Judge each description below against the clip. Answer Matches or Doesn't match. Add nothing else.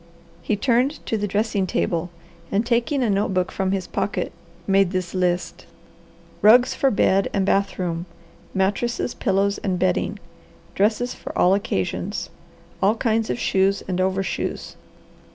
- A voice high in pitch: Matches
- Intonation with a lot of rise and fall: Doesn't match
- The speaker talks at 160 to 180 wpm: Doesn't match